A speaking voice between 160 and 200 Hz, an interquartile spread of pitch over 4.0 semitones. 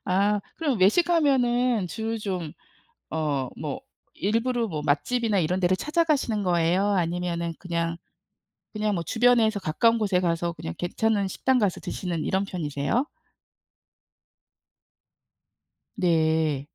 Yes: high, 190 Hz; average, 5.3 semitones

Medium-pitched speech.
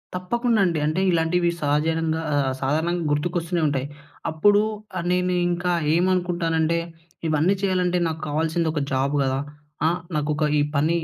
Yes: medium, 165 Hz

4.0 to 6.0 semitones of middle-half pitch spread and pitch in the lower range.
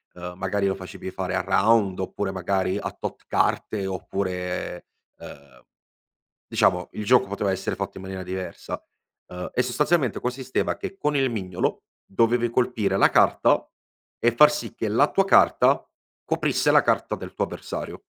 Yes: average, 4.4 semitones; low, 100 Hz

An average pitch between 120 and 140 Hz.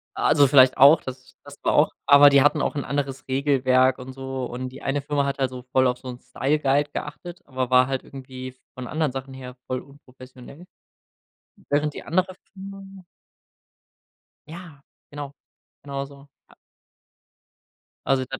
Yes: low, 135 Hz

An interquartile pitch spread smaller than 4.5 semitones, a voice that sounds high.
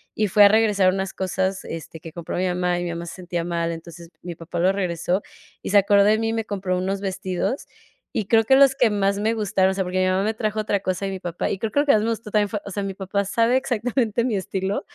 Yes: average, 2.9 semitones; high, 195 Hz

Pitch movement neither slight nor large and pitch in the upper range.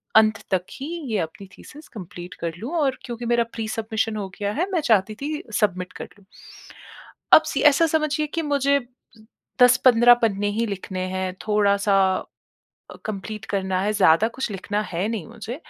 Yes: average, 4.1 semitones; high, 215 Hz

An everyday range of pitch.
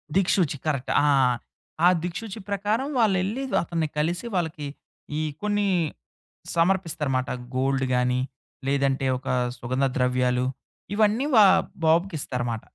No: wide, 6.7 semitones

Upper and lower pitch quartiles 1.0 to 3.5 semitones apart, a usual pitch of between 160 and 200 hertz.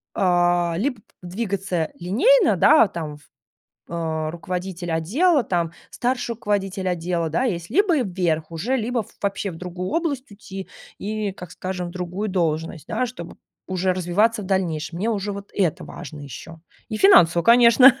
No: average, 4.1 semitones; medium, 185 Hz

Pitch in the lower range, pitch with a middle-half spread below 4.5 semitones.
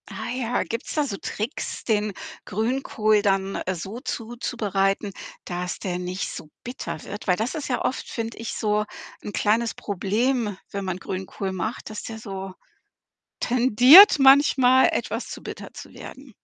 No: high, 215 Hz; average, 4.1 semitones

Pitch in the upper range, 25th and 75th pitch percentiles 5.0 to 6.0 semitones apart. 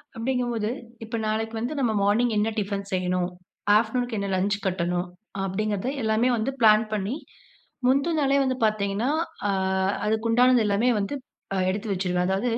No: high, 215 Hz; average, 3.4 semitones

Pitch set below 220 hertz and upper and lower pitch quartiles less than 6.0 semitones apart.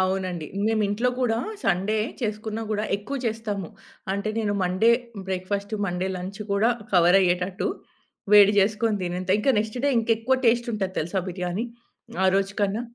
Yes: high, 200 Hz; average, 2.9 semitones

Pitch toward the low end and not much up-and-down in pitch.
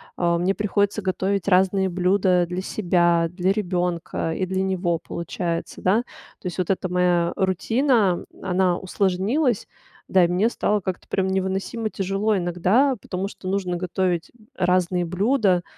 No: medium, 185 Hz; narrow, 1.8 semitones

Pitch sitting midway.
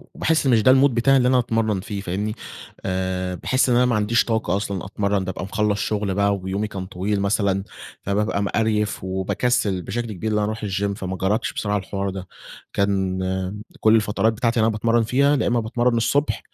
No: low, 105 Hz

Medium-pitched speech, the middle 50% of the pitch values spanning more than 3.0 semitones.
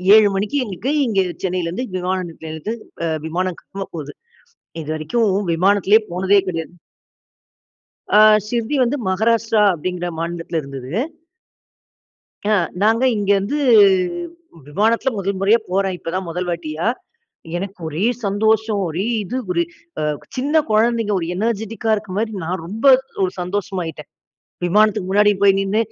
No: high, 195 Hz; average, 3.6 semitones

